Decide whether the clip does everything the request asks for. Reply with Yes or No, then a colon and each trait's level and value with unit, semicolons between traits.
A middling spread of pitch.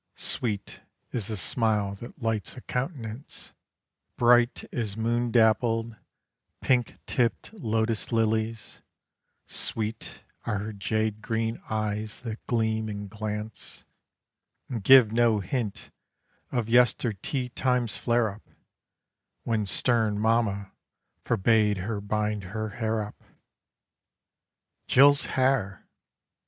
No: narrow, 2.0 semitones